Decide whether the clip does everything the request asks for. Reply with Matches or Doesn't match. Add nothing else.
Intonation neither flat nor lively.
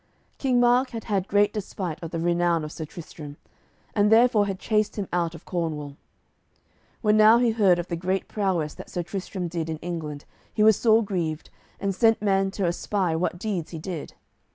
Matches